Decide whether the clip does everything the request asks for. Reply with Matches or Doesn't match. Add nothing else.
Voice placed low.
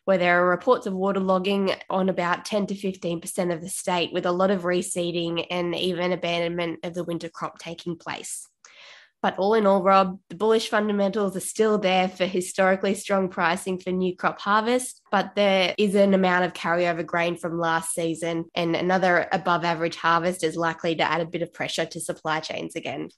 Doesn't match